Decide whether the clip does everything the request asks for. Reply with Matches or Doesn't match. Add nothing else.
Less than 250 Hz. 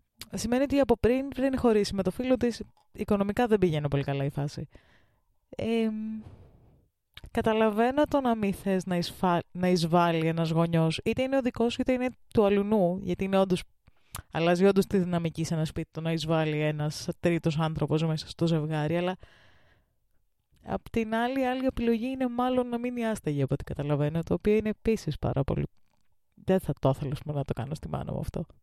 Matches